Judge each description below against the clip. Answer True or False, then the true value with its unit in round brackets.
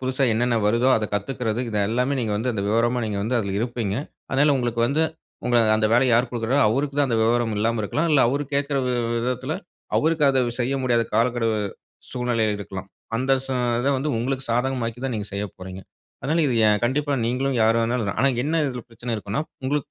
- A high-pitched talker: False (120 Hz)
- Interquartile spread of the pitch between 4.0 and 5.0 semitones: False (2.9 semitones)